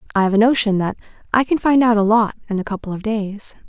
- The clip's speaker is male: No, female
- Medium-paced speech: No, fast, 260 wpm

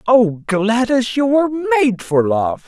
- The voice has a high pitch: Yes, high, 230 Hz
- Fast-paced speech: No, average, 155 wpm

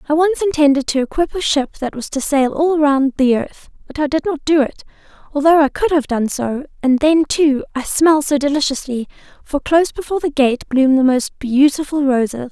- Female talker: Yes, female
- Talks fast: Yes, fast, 210 wpm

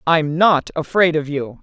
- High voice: No, medium, 160 Hz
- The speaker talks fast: No, average, 185 wpm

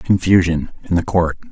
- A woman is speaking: No, male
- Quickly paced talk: No, average, 160 wpm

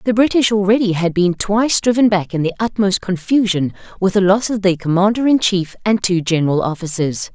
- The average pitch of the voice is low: No, high, 195 Hz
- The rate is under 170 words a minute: No, average, 195 wpm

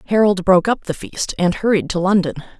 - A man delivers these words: No, female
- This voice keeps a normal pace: No, fast, 210 wpm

